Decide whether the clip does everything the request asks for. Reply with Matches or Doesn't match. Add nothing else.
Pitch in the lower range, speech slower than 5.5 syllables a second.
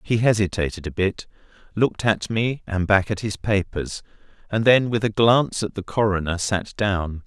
Matches